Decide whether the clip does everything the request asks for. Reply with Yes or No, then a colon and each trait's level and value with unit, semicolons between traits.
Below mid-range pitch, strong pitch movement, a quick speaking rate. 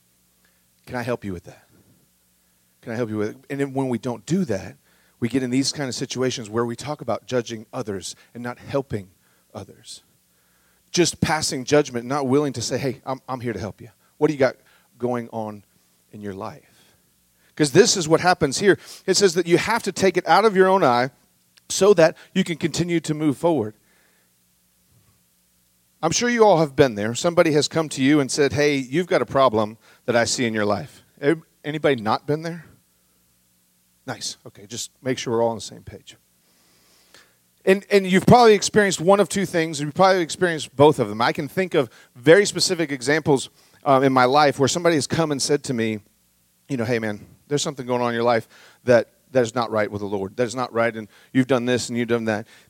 Yes: low, 130 Hz; wide, 6.4 semitones; fast, 215 wpm